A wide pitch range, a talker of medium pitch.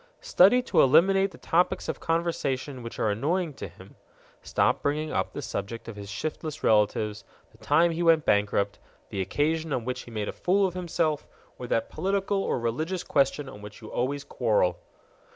Yes: wide, 7.6 semitones; medium, 145 Hz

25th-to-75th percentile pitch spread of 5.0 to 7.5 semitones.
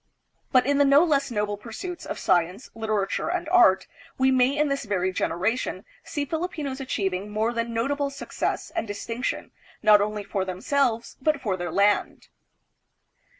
Yes: wide, 5.5 semitones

